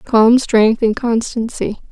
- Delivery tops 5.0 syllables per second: No, 3.6 syllables/s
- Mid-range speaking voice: No, high, 230 Hz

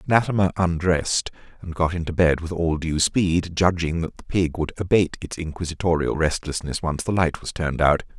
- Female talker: No, male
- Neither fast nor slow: Yes, average, 185 wpm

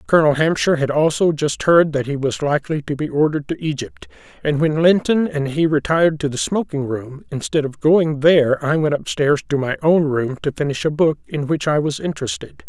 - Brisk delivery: Yes, fast, 215 wpm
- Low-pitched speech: No, medium, 150 Hz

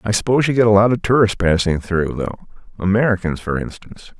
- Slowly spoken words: No, average, 200 wpm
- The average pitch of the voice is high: No, low, 100 Hz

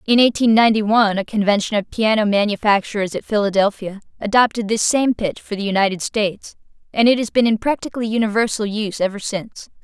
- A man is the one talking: No, female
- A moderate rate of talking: Yes, average, 175 wpm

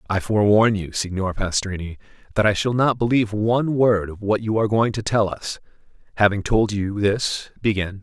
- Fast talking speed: No, average, 185 wpm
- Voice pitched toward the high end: No, low, 105 Hz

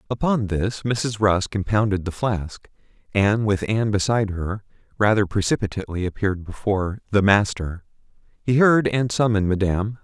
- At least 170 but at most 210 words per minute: No, average, 140 wpm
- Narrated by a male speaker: Yes, male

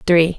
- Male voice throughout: No, female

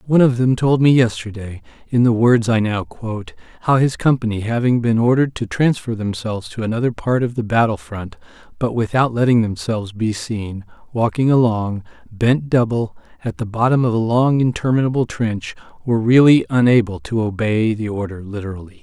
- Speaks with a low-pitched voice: Yes, low, 115 Hz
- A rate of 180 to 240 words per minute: No, average, 165 wpm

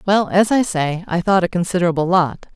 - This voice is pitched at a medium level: Yes, medium, 180 Hz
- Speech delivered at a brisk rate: Yes, fast, 210 wpm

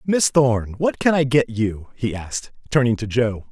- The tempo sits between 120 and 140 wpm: No, fast, 205 wpm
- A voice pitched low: Yes, low, 125 Hz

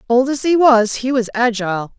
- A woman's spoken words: Yes, female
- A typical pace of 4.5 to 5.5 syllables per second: Yes, 5.0 syllables/s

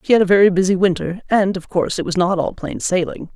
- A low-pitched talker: No, medium, 185 Hz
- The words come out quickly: Yes, fast, 270 wpm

